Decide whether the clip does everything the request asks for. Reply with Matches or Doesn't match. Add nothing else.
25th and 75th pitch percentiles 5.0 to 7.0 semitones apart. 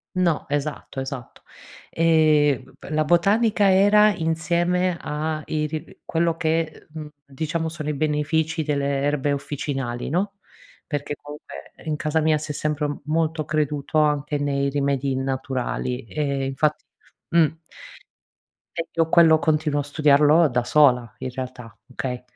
Doesn't match